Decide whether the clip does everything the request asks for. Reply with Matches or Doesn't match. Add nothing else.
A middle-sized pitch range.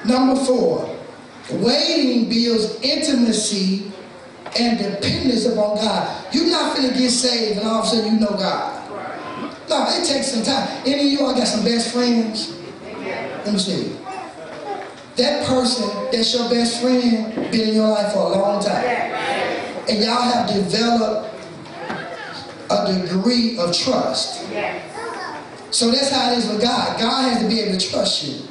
Matches